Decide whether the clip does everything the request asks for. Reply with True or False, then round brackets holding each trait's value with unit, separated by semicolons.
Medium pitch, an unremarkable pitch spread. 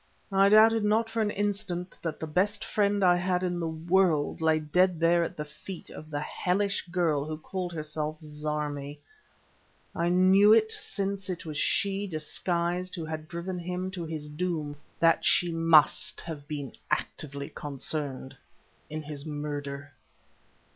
True (170 Hz; 3.7 semitones)